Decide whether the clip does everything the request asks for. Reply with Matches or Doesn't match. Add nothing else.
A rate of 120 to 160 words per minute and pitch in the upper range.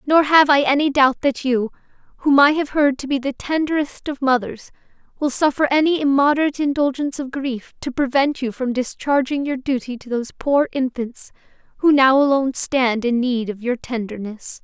Doesn't match